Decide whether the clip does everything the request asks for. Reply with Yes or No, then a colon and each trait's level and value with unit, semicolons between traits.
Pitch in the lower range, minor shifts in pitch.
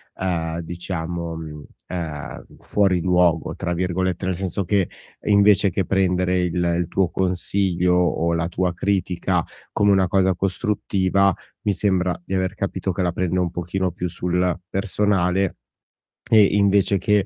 Yes: very low, 90 Hz; narrow, 1.8 semitones